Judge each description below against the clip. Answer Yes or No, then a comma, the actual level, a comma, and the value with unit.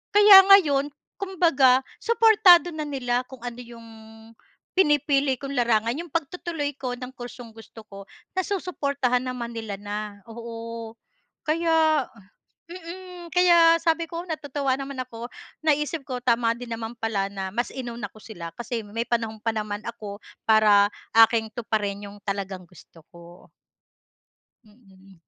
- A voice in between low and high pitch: No, high, 245 Hz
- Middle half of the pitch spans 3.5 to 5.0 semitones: No, wide, 5.6 semitones